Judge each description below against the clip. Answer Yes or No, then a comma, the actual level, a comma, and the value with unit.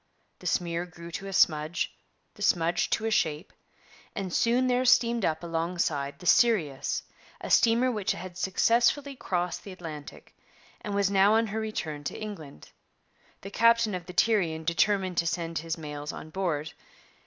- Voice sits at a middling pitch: Yes, medium, 180 Hz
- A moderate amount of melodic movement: Yes, average, 4.9 semitones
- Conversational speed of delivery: Yes, average, 165 wpm